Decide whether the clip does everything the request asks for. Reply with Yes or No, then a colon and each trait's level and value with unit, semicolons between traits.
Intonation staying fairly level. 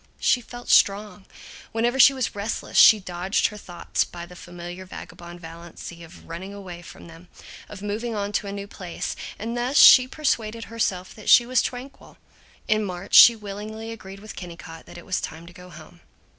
No: average, 4.2 semitones